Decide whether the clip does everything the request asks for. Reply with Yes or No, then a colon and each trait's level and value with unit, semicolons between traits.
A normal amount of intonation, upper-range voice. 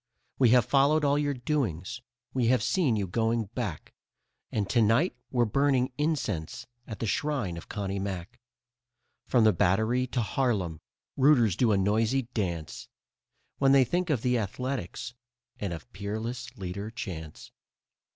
No: average, 4.6 semitones; low, 115 Hz